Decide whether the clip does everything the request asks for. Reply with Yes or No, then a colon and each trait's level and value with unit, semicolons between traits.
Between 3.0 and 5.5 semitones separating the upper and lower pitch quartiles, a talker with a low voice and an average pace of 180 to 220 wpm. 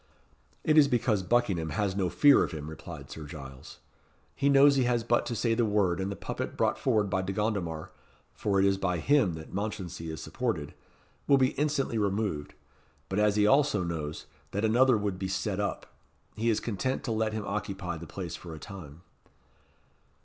Yes: average, 5.0 semitones; low, 100 Hz; average, 195 wpm